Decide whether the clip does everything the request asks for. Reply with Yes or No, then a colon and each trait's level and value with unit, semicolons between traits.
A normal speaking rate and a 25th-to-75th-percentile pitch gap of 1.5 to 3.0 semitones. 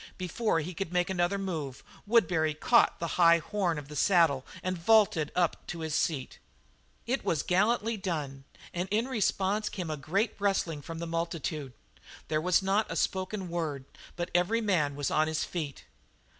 No: average, 170 wpm; average, 3.8 semitones